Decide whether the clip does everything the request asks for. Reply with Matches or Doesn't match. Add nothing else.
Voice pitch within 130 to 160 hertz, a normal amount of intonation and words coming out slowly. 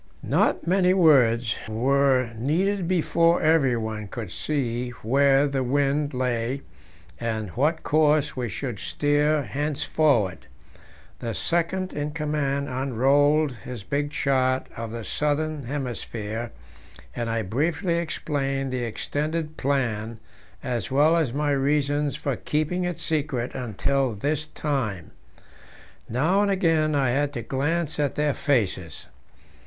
Matches